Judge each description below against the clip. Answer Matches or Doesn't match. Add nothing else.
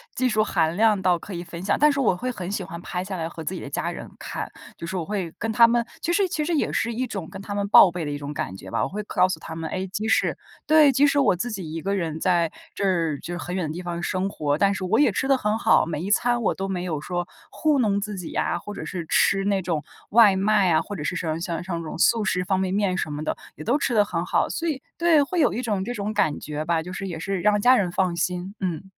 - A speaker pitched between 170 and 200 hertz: Matches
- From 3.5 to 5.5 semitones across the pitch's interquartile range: Matches